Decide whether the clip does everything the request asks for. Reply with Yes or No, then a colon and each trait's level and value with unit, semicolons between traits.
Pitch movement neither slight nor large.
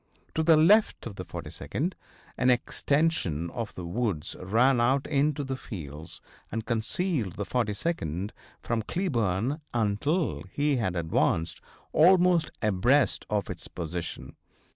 No: wide, 8.3 semitones